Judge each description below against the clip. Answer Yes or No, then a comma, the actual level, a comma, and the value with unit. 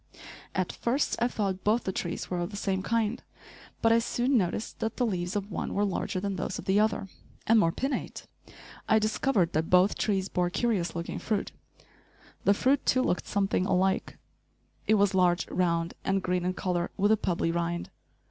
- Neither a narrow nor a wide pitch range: Yes, average, 3.3 semitones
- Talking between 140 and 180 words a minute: No, average, 190 wpm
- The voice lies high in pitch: Yes, high, 195 Hz